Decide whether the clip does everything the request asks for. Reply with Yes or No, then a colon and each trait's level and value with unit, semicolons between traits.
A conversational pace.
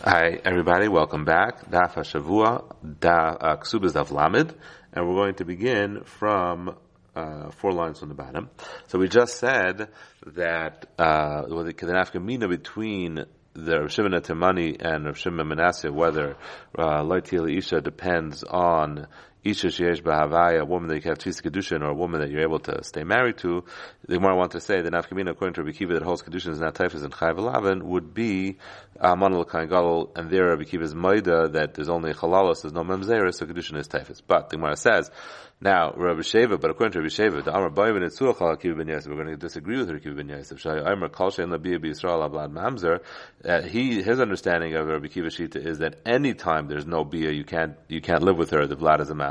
Yes: average, 195 wpm